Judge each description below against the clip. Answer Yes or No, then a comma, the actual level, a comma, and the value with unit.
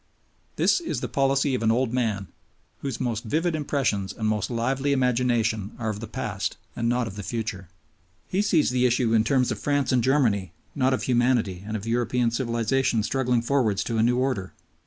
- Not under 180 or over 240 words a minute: Yes, average, 195 wpm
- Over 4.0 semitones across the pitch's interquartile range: No, average, 3.1 semitones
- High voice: No, low, 120 Hz